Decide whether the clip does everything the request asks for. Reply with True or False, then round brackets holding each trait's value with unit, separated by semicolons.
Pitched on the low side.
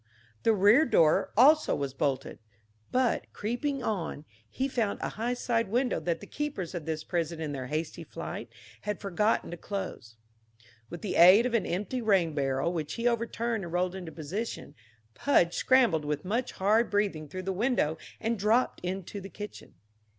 False (195 Hz)